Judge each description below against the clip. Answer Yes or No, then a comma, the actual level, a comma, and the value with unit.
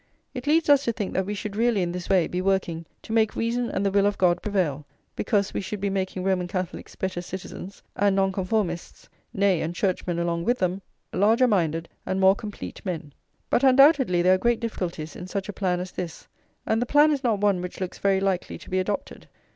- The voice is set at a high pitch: Yes, high, 195 Hz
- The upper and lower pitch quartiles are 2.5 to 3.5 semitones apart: Yes, average, 3.0 semitones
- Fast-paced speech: Yes, fast, 220 wpm